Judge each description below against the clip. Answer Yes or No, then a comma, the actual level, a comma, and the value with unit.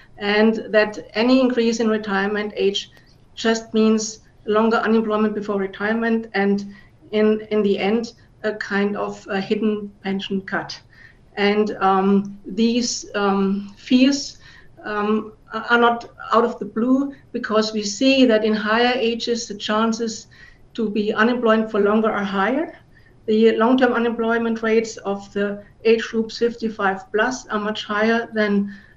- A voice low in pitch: No, high, 215 Hz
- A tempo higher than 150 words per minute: No, average, 140 wpm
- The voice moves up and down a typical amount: No, narrow, 2.0 semitones